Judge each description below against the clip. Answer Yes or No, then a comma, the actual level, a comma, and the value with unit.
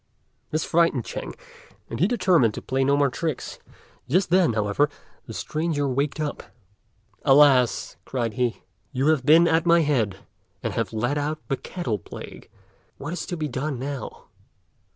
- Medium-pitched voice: Yes, medium, 145 Hz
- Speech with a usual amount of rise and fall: Yes, average, 4.1 semitones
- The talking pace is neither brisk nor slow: Yes, average, 160 wpm